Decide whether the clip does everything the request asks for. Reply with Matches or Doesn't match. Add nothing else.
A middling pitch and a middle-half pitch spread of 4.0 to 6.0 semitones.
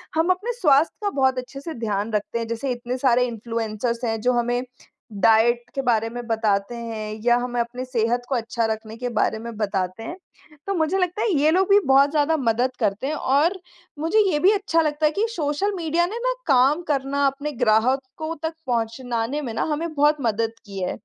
Doesn't match